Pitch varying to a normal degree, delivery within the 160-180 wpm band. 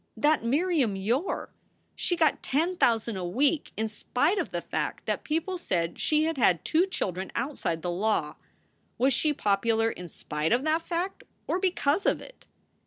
No: wide, 7.8 semitones; average, 175 wpm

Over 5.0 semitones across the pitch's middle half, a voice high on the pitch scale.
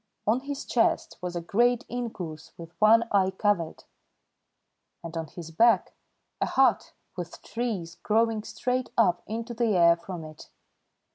Yes: wide, 5.5 semitones; high, 205 Hz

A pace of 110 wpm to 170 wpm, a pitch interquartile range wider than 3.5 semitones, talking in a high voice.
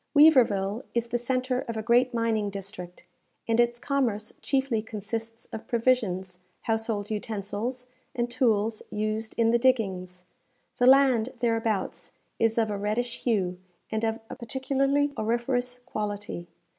No: slow, 135 wpm; average, 2.8 semitones; high, 225 Hz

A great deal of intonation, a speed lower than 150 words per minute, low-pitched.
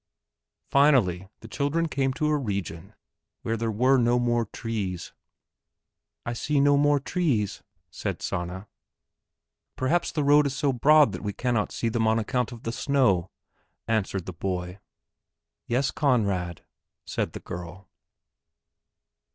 Yes: wide, 6.2 semitones; slow, 135 wpm; low, 115 Hz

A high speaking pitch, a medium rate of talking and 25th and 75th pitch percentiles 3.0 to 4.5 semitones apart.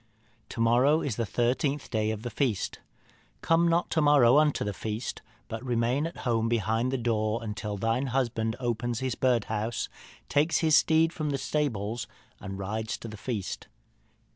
No: low, 120 Hz; average, 165 wpm; average, 4.1 semitones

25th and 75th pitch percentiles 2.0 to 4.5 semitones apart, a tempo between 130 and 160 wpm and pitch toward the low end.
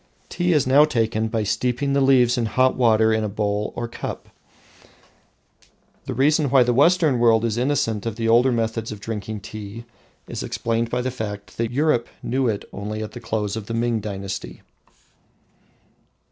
No: average, 2.8 semitones; average, 175 wpm; low, 115 Hz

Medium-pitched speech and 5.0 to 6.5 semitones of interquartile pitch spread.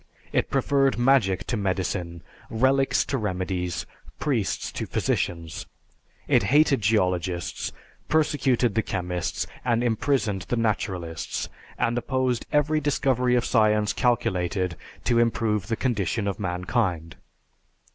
No: low, 110 Hz; wide, 5.4 semitones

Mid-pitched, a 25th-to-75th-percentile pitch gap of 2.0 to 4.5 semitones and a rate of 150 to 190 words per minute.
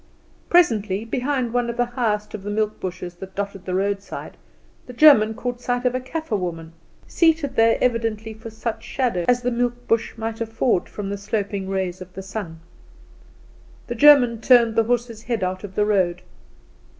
No: high, 225 Hz; average, 3.8 semitones; average, 180 wpm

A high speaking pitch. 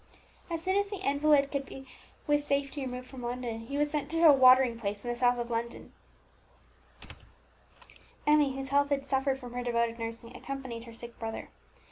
Yes: very high, 265 Hz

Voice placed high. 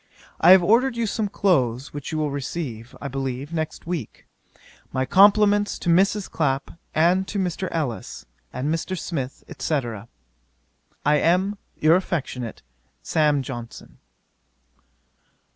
No: medium, 160 Hz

